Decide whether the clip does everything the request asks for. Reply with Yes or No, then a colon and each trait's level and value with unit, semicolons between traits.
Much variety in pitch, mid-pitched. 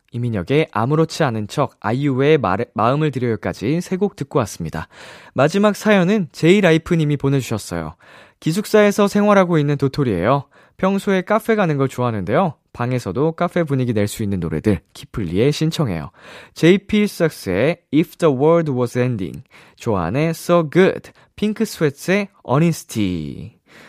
Yes: wide, 6.0 semitones; medium, 150 Hz